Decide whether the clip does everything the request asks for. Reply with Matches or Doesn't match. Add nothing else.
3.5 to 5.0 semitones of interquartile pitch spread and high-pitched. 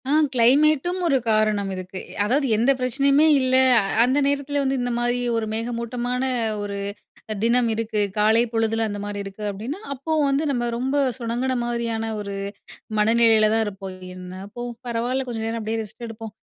Doesn't match